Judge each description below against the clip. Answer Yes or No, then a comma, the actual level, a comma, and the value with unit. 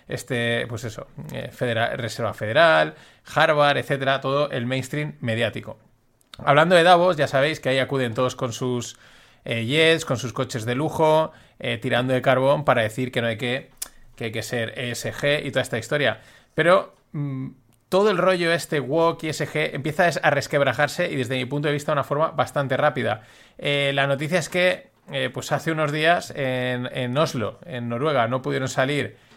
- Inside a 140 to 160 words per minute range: No, average, 185 wpm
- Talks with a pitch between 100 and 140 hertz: Yes, low, 135 Hz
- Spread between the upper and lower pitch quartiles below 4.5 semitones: Yes, average, 3.4 semitones